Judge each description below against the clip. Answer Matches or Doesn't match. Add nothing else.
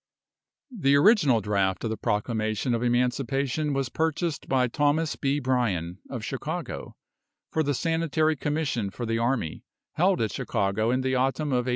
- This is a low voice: Matches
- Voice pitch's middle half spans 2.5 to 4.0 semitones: Doesn't match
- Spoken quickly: Doesn't match